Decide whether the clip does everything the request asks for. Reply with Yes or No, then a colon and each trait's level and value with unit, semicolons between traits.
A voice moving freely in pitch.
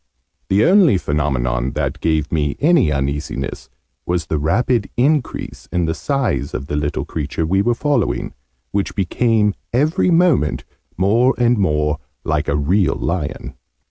Yes: wide, 8.4 semitones